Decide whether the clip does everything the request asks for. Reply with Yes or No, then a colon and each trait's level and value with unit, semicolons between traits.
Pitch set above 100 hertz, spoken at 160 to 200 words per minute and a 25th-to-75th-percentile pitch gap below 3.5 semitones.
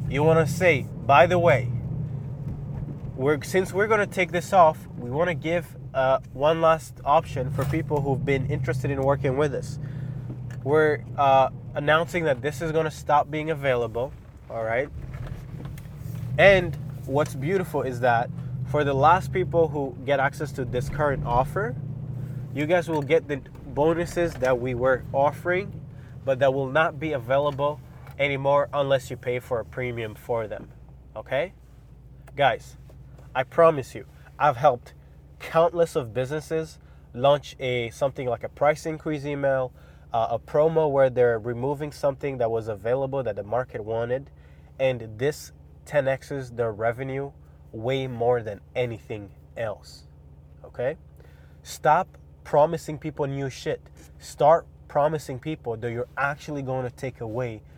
No: low, 135 Hz; average, 145 wpm; average, 3.0 semitones